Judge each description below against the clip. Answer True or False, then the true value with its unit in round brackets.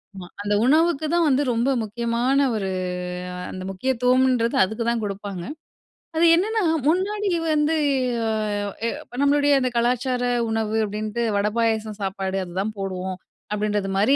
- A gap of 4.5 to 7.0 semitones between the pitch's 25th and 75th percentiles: True (5.0 semitones)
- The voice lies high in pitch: True (230 Hz)